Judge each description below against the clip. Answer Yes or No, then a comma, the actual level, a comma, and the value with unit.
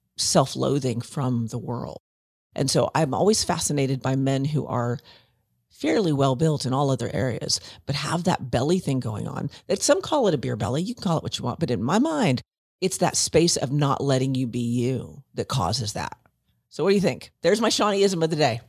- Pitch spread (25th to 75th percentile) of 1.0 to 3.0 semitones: No, average, 4.7 semitones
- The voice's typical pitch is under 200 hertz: Yes, low, 135 Hz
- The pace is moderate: No, fast, 220 wpm